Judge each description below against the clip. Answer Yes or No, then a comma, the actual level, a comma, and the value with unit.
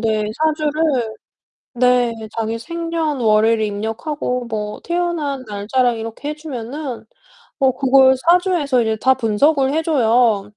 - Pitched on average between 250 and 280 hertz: Yes, very high, 255 Hz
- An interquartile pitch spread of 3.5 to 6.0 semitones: Yes, average, 5.1 semitones